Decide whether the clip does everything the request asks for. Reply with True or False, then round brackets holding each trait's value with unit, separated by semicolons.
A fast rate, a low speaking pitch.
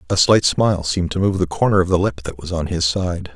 True (285 wpm; 90 Hz)